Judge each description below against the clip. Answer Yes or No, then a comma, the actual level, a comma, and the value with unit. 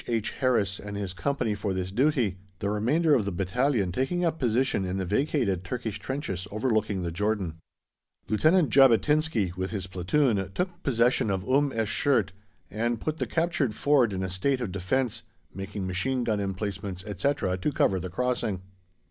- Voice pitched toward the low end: Yes, low, 110 Hz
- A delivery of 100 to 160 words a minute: No, average, 170 wpm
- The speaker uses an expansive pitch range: Yes, wide, 5.7 semitones